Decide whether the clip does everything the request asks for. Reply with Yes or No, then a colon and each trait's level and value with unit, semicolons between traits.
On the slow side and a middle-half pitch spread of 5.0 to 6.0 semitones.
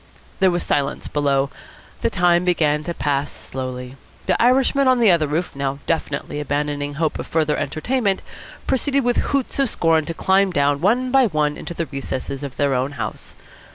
No: average, 180 wpm; wide, 5.4 semitones